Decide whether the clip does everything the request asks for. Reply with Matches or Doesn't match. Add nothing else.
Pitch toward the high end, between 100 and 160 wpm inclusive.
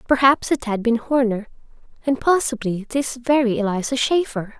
Matches